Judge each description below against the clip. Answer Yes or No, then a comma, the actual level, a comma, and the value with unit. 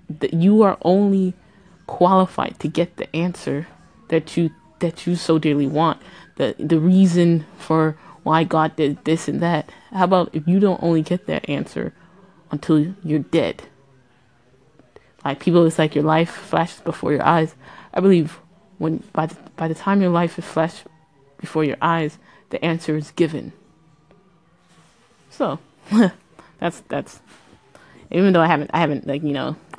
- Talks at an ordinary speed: Yes, average, 155 wpm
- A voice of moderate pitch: Yes, medium, 165 Hz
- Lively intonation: No, narrow, 2.5 semitones